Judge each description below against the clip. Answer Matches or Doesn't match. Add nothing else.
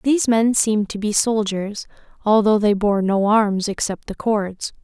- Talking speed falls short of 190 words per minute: Matches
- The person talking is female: Matches